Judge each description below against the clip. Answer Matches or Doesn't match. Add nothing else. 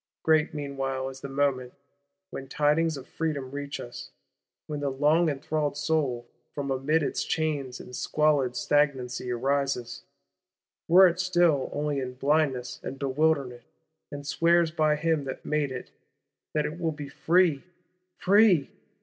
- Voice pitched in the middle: Matches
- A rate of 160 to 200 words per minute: Doesn't match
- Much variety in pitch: Doesn't match